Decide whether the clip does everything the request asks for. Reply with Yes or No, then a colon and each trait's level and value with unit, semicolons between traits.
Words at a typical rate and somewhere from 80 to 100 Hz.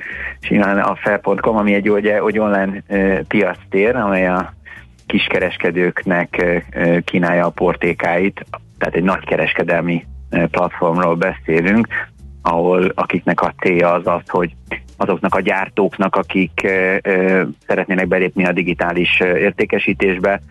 Yes: average, 115 wpm; very low, 90 Hz